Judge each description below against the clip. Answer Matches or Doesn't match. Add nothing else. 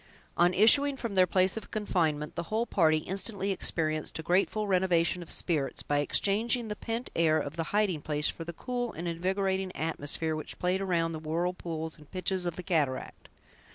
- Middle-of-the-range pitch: Matches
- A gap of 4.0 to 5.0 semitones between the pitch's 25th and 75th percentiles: Doesn't match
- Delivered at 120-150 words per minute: Doesn't match